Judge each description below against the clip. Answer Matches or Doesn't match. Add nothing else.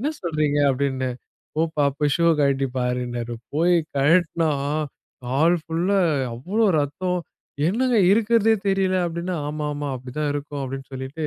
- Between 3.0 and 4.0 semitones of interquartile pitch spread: Doesn't match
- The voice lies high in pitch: Doesn't match